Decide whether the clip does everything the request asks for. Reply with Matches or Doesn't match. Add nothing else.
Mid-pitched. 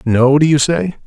Matches